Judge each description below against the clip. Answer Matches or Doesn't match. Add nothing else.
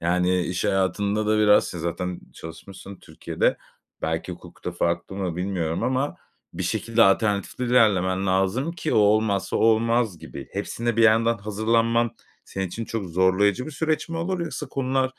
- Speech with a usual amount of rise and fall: Matches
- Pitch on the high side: Doesn't match